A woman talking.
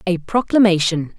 Yes: female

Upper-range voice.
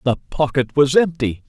No: medium, 140 Hz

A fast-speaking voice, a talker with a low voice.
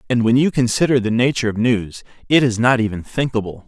Yes: fast, 210 wpm; low, 120 Hz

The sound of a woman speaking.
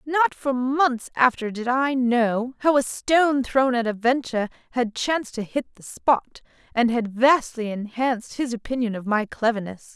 Yes: female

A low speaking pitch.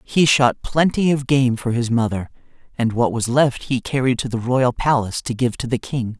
Yes: low, 125 Hz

